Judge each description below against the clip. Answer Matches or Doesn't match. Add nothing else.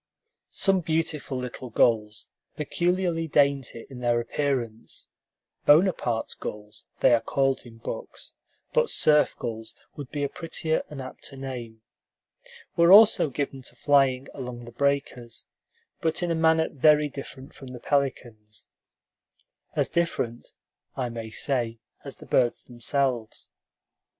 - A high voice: Doesn't match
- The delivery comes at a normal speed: Doesn't match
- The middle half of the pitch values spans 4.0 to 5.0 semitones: Matches